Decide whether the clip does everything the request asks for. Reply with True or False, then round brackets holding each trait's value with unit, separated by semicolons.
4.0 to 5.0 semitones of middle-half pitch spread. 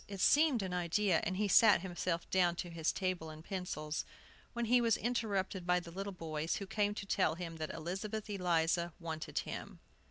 False (3.3 semitones)